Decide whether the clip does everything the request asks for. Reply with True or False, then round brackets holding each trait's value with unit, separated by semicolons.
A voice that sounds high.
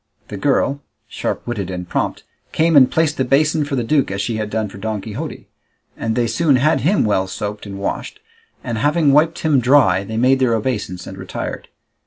False (120 Hz)